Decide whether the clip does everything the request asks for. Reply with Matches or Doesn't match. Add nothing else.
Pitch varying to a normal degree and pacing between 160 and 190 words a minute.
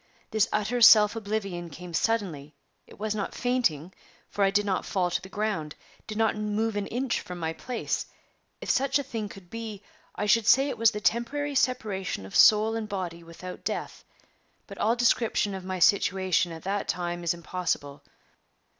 Matches